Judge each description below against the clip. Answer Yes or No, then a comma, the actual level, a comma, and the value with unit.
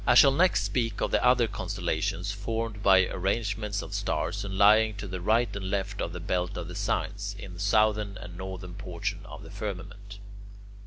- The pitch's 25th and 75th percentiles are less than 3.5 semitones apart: Yes, narrow, 2.4 semitones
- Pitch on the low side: Yes, low, 100 Hz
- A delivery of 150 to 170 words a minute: No, average, 195 wpm